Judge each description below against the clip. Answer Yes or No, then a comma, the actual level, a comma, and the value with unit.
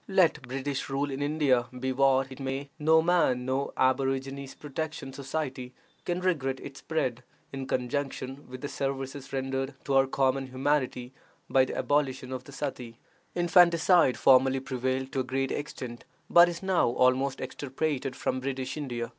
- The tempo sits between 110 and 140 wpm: No, average, 155 wpm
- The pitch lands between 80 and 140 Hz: Yes, low, 135 Hz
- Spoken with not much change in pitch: Yes, narrow, 1.8 semitones